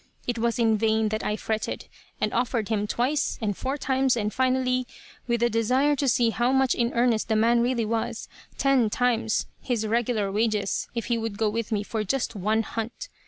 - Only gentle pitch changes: Yes, narrow, 2.3 semitones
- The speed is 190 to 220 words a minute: Yes, average, 200 wpm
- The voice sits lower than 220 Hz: No, high, 230 Hz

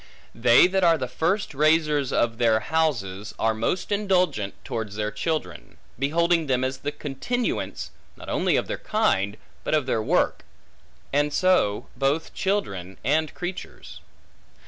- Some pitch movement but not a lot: No, wide, 7.0 semitones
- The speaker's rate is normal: Yes, average, 145 wpm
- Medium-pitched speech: Yes, medium, 145 Hz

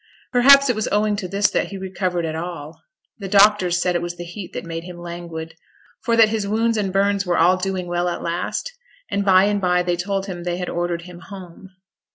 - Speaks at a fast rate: Yes, fast, 225 wpm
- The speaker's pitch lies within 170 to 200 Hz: Yes, medium, 185 Hz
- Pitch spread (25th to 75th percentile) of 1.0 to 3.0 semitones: Yes, narrow, 2.6 semitones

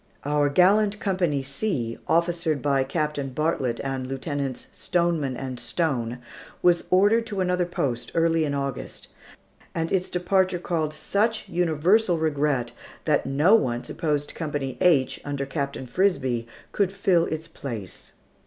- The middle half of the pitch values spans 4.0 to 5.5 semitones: Yes, average, 4.7 semitones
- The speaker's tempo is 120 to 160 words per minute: Yes, slow, 135 wpm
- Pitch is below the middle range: No, medium, 155 Hz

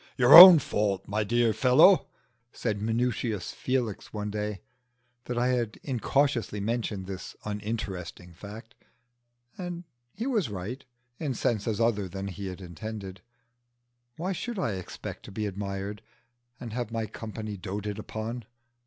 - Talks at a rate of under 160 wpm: Yes, slow, 135 wpm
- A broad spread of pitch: No, average, 3.5 semitones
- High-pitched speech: No, low, 110 Hz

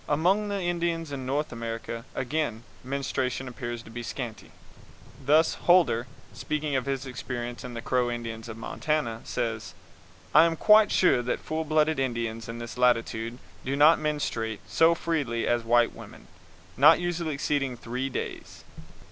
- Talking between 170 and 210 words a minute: No, average, 155 wpm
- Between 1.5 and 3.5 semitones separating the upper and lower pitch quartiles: No, average, 4.8 semitones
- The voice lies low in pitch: Yes, low, 130 Hz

